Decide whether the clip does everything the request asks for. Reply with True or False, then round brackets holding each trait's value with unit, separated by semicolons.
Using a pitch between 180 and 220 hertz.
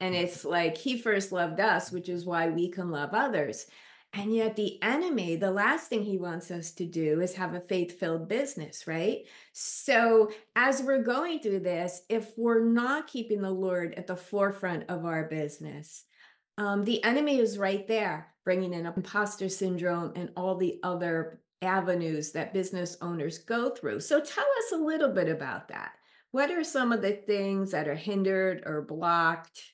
True (190 Hz)